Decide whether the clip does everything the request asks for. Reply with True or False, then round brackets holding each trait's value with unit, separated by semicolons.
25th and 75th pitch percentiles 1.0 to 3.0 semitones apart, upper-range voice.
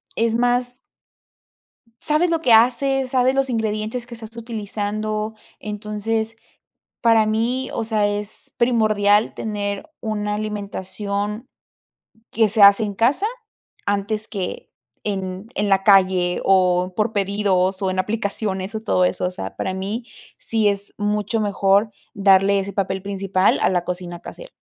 True (2.4 semitones; 210 Hz)